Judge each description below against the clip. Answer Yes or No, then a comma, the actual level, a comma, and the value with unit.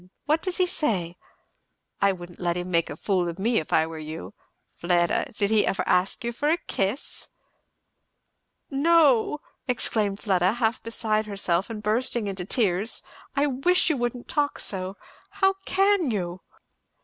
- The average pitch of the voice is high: Yes, high, 215 Hz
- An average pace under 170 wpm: Yes, average, 160 wpm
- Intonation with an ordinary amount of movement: No, wide, 7.0 semitones